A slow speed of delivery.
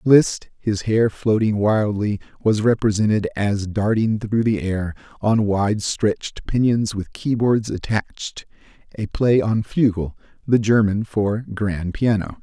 Yes: slow, 130 wpm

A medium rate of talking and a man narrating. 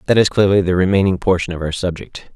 No: fast, 230 wpm; male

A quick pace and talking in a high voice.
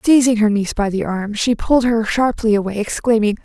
Yes: fast, 210 wpm; high, 220 Hz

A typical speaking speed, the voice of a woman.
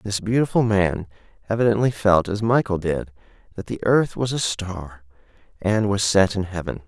No: average, 165 wpm; male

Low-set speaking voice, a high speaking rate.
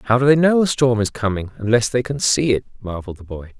Yes: low, 120 Hz; fast, 265 wpm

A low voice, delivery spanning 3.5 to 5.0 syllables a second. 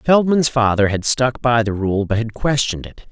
Yes: low, 120 Hz; 4.9 syllables/s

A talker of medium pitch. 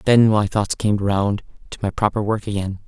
No: low, 105 Hz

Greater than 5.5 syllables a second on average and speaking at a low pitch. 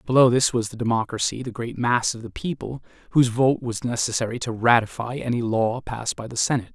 Yes: 6.1 syllables/s; low, 120 Hz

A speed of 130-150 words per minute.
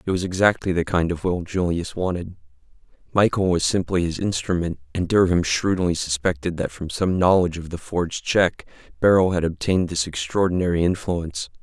No: average, 165 wpm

